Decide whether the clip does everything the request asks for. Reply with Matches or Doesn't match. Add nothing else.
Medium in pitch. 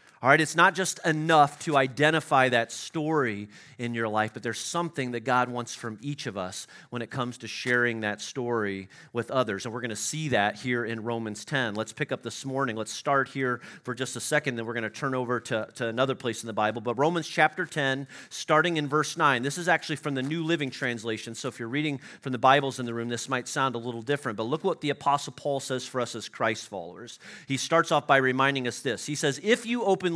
Doesn't match